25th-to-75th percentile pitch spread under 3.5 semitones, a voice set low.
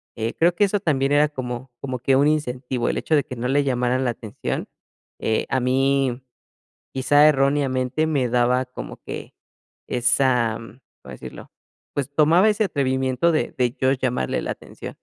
Yes: average, 2.7 semitones; low, 130 Hz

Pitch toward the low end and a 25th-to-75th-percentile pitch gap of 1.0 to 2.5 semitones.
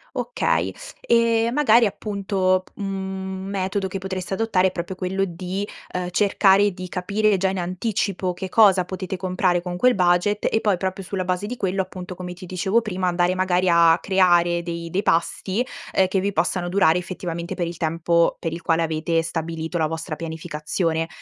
No: medium, 185 Hz; narrow, 2.1 semitones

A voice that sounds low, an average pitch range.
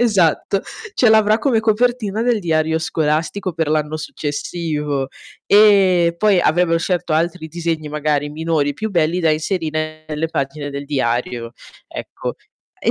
No: medium, 160 Hz; average, 4.1 semitones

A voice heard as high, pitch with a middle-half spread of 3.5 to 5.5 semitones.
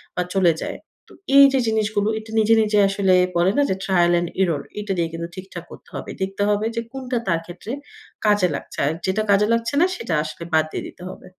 Yes: high, 195 Hz; average, 3.8 semitones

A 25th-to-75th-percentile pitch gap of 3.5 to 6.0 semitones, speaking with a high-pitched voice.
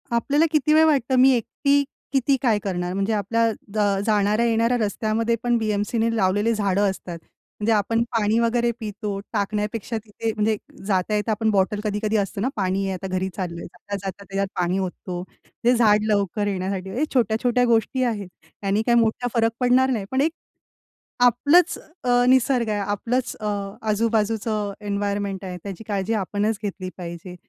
No: average, 2.9 semitones; high, 215 Hz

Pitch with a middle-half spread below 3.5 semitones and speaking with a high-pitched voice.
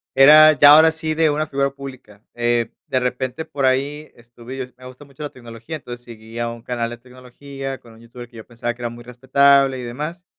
No: average, 2.8 semitones; low, 130 Hz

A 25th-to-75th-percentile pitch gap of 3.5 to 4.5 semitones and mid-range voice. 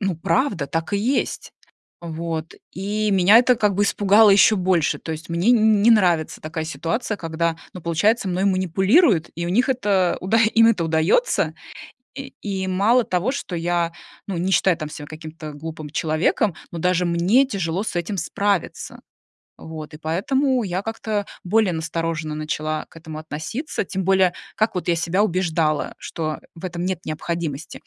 Yes: average, 4.0 semitones; medium, 180 Hz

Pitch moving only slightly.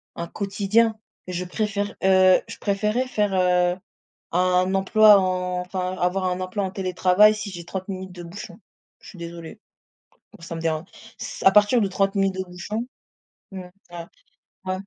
Yes: narrow, 2.0 semitones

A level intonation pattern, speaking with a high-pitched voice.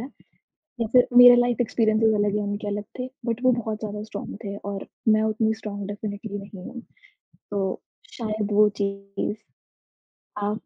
Yes: narrow, 1.7 semitones; high, 215 Hz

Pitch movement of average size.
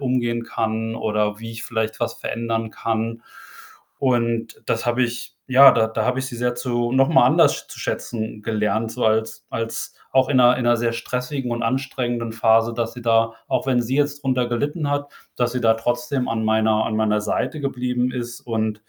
No: narrow, 1.9 semitones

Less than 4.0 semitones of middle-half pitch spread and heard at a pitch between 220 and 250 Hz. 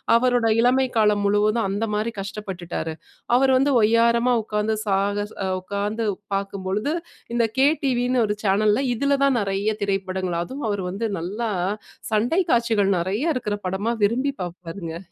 No: average, 3.3 semitones; high, 210 Hz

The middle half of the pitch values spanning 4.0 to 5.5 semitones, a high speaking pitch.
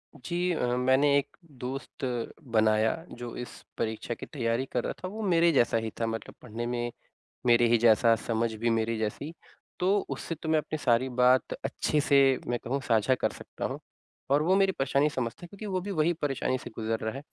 No: average, 4.5 semitones; low, 125 Hz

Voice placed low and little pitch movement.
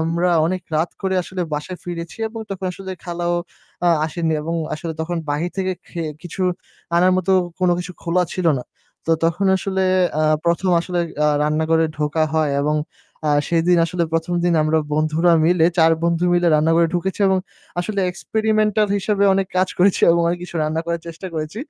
No: medium, 175 Hz; narrow, 2.3 semitones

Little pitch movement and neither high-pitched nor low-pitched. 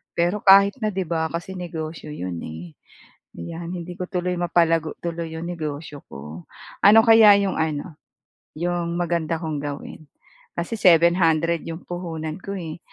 Yes: narrow, 2.3 semitones; medium, 170 Hz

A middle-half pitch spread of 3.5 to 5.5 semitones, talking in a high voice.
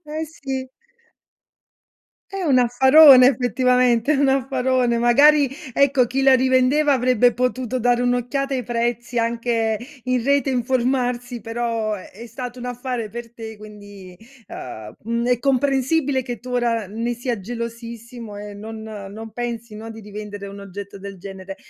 No: narrow, 2.6 semitones; high, 240 Hz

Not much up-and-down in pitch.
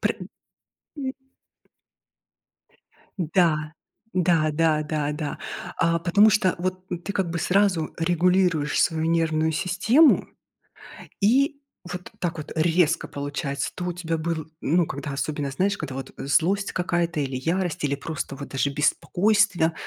No: average, 3.1 semitones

